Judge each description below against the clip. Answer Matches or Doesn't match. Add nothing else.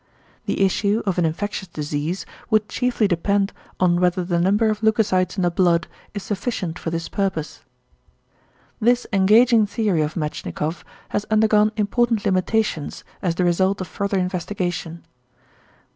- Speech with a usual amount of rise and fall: Matches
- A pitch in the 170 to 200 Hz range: Matches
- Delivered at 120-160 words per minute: Matches